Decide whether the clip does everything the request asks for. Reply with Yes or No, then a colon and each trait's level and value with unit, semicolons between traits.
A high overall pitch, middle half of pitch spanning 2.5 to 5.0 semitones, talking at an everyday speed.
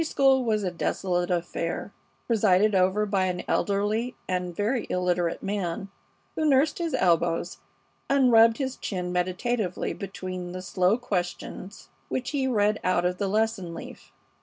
Yes: high, 195 Hz; average, 4.1 semitones; average, 155 wpm